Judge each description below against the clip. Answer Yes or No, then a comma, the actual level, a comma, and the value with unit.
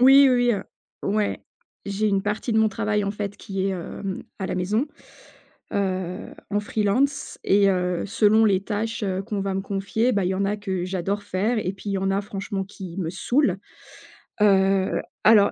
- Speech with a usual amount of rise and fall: No, narrow, 1.9 semitones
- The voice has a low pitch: No, high, 200 Hz